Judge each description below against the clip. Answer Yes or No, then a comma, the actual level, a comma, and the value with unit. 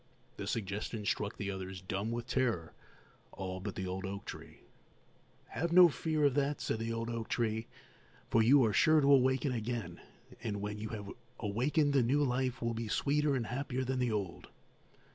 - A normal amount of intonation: Yes, average, 4.4 semitones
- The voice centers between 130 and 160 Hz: No, low, 115 Hz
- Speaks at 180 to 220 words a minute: Yes, average, 185 wpm